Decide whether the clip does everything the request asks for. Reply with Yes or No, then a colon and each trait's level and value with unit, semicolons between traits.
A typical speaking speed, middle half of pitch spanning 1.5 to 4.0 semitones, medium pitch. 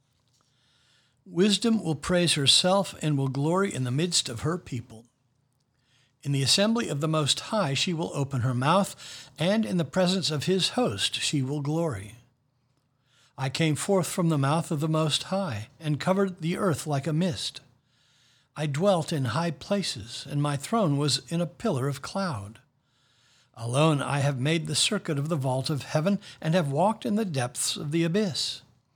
No: average, 180 wpm; average, 4.8 semitones; medium, 145 Hz